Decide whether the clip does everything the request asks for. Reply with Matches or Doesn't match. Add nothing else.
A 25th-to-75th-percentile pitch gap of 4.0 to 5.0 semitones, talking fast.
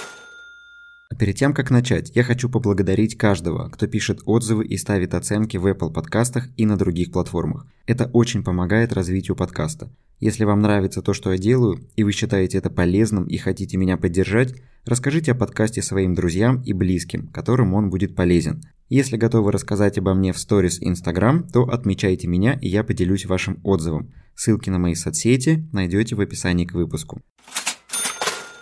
Matches